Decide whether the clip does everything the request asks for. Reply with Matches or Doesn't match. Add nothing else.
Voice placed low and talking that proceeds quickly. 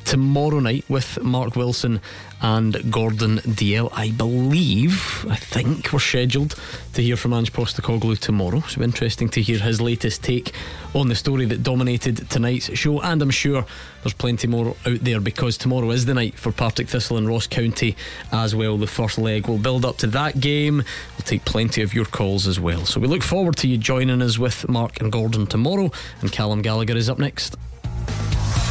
Doesn't match